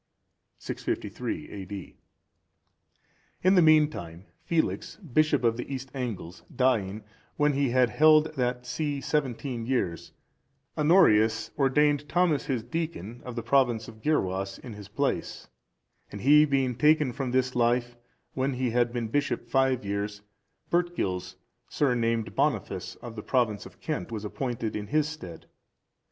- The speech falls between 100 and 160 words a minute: Yes, average, 140 wpm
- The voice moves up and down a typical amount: Yes, average, 4.9 semitones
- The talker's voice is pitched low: Yes, low, 125 Hz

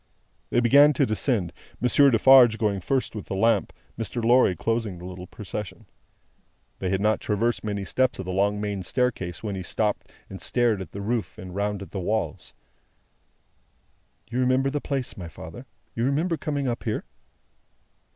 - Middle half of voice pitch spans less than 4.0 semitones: No, average, 4.4 semitones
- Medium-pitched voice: No, low, 110 Hz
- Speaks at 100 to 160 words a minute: No, average, 170 wpm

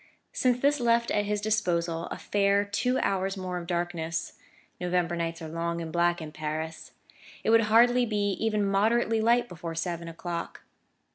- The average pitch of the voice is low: No, high, 190 Hz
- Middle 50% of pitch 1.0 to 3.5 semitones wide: No, average, 4.5 semitones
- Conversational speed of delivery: Yes, average, 160 wpm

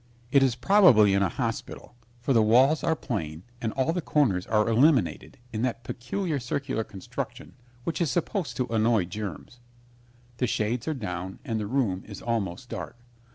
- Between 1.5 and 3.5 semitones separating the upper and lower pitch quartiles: No, average, 4.5 semitones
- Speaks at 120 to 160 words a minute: No, average, 170 wpm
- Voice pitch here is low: Yes, low, 115 Hz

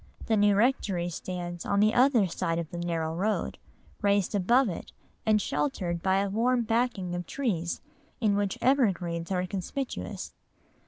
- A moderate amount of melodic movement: Yes, average, 4.3 semitones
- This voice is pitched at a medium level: No, high, 195 Hz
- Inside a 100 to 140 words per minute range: No, average, 155 wpm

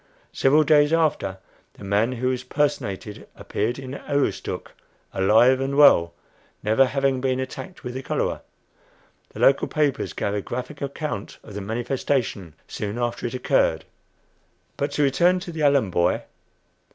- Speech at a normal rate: Yes, average, 150 wpm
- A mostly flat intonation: No, average, 4.5 semitones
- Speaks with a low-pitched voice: Yes, low, 130 Hz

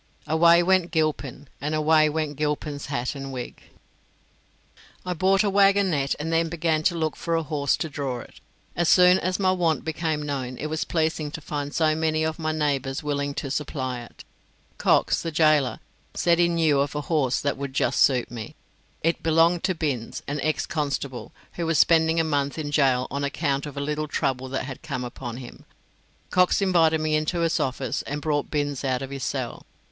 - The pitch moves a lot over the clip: No, average, 2.7 semitones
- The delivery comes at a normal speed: Yes, average, 195 wpm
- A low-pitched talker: No, medium, 150 Hz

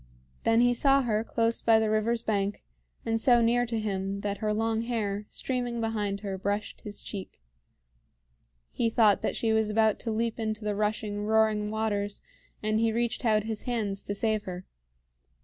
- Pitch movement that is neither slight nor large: No, narrow, 1.7 semitones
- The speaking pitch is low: No, high, 220 Hz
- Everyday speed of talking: Yes, average, 180 wpm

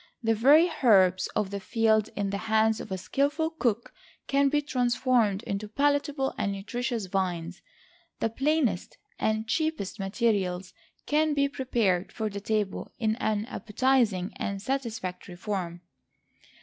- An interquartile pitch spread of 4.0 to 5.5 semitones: Yes, average, 5.0 semitones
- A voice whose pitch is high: Yes, high, 220 Hz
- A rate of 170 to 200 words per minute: No, slow, 135 wpm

